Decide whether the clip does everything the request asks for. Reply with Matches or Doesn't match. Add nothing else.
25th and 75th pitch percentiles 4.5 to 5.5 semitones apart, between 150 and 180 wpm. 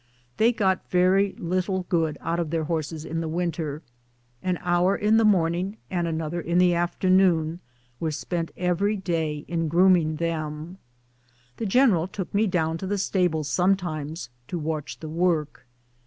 Doesn't match